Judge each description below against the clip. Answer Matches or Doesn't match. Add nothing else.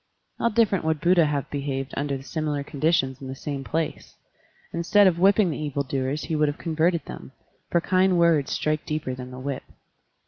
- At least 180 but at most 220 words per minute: Matches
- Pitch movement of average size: Matches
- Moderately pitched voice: Matches